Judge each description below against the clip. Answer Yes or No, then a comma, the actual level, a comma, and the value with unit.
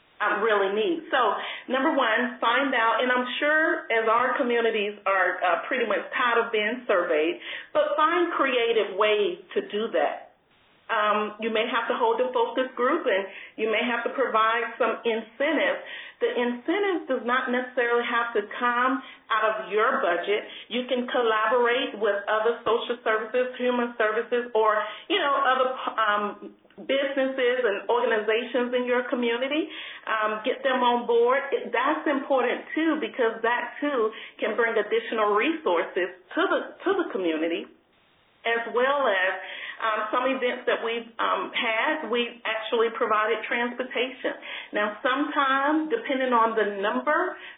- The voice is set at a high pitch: Yes, high, 240 Hz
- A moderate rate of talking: Yes, average, 150 wpm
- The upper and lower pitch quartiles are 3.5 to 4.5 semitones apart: Yes, average, 3.9 semitones